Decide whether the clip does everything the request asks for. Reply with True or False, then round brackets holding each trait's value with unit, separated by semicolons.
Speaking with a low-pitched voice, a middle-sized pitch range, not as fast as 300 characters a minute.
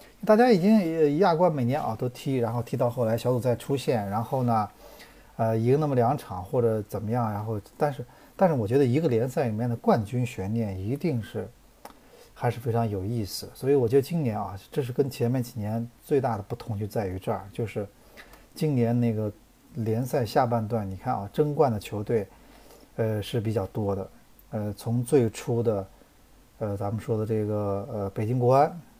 True (115 Hz; 3.3 semitones; 280 characters per minute)